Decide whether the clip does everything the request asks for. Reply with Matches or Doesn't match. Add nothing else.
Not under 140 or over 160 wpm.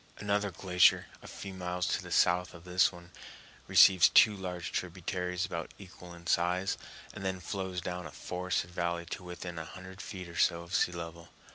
Doesn't match